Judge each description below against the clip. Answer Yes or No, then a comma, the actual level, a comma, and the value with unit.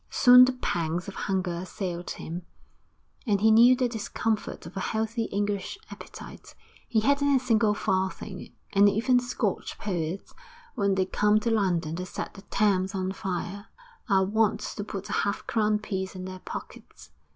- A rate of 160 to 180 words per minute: Yes, average, 165 wpm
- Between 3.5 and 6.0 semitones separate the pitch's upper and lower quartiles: No, average, 2.9 semitones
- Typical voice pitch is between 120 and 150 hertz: No, high, 200 Hz